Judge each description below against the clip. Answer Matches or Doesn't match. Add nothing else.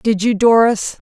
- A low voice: Doesn't match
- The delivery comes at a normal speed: Matches